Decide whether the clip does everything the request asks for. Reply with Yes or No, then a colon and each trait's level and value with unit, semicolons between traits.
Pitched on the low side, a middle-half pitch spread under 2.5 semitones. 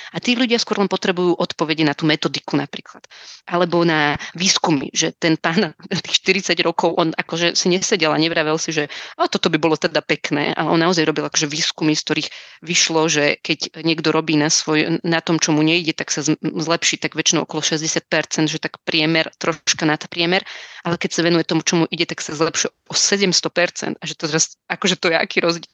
No: medium, 165 Hz; narrow, 2.0 semitones